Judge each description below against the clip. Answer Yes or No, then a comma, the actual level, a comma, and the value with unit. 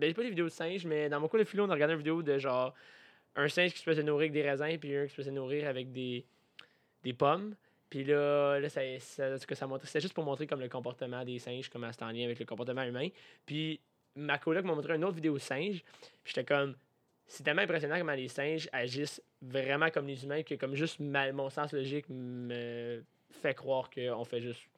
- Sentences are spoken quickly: Yes, fast, 230 wpm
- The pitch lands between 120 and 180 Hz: Yes, medium, 140 Hz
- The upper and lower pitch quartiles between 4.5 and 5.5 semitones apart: No, average, 3.0 semitones